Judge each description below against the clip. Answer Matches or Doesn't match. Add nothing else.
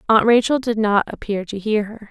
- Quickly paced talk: Matches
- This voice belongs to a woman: Matches